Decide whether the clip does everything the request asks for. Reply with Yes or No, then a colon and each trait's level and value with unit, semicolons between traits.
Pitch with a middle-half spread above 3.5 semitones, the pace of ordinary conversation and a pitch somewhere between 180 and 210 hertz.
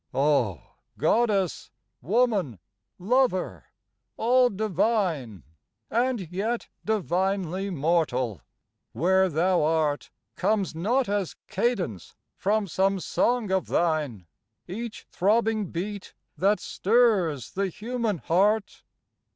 No: average, 4.9 semitones; slow, 95 wpm; high, 190 Hz